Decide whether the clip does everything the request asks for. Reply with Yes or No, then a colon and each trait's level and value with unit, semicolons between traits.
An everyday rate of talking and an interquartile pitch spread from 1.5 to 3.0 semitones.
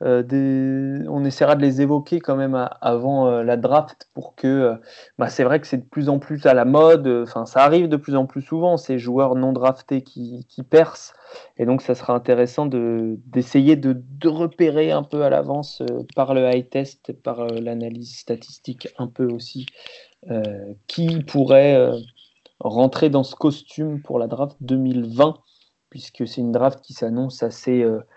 Yes: average, 190 wpm; average, 2.7 semitones